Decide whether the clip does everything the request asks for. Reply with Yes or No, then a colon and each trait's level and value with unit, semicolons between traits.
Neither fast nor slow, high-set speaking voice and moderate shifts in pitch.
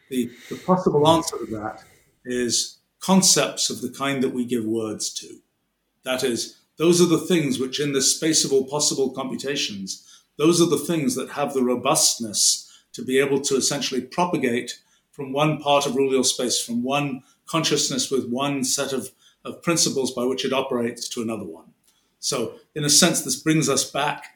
No: average, 180 wpm; low, 135 Hz; average, 3.5 semitones